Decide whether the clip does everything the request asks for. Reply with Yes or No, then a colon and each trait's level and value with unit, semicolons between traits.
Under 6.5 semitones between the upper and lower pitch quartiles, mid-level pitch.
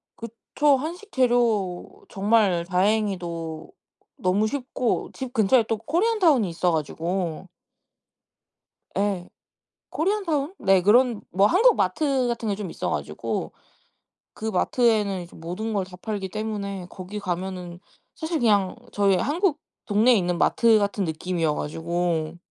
No: average, 5.2 semitones; high, 205 Hz